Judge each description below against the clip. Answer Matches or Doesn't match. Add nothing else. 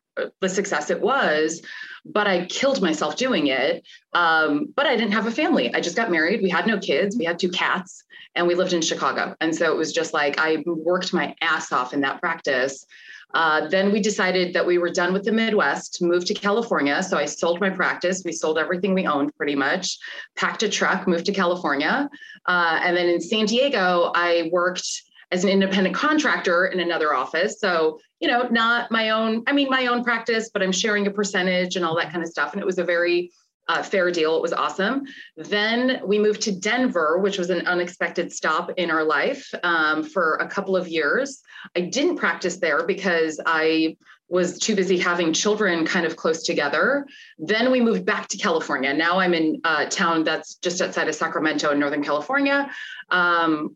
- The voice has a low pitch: Doesn't match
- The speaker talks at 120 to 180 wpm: Doesn't match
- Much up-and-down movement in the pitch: Doesn't match